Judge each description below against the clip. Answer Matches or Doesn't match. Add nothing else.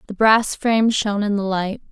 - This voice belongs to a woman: Matches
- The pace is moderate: Doesn't match